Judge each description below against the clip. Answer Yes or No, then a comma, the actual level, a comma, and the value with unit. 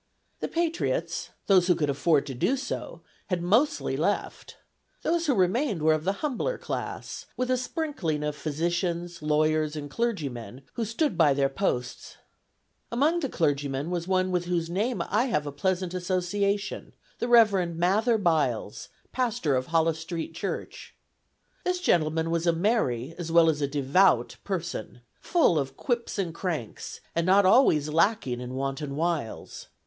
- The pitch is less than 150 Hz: No, medium, 170 Hz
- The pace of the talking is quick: No, average, 155 wpm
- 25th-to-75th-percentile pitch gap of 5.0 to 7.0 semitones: Yes, wide, 5.6 semitones